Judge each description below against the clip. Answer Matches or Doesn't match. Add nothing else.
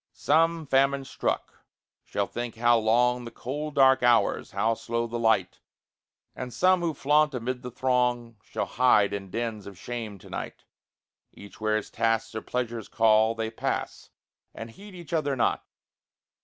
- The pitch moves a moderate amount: Matches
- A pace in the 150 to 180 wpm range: Matches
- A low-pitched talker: Matches